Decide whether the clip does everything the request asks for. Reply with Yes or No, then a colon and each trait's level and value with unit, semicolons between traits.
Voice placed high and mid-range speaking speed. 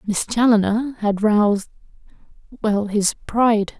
No: high, 215 Hz; slow, 95 wpm